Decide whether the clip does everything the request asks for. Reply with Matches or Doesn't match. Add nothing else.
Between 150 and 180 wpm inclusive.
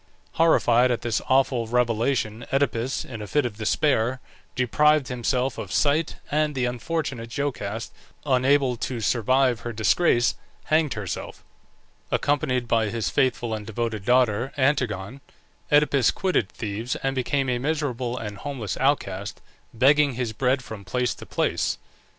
Doesn't match